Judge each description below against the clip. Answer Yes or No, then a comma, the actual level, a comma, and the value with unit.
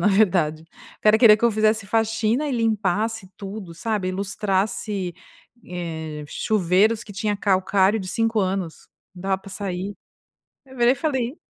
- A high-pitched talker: Yes, high, 205 Hz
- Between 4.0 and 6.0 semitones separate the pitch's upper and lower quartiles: No, average, 2.9 semitones